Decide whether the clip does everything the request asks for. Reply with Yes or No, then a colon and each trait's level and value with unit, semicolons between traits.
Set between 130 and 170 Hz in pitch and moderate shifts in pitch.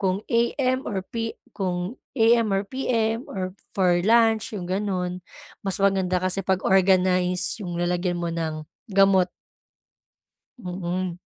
No: high, 190 Hz; average, 3.2 semitones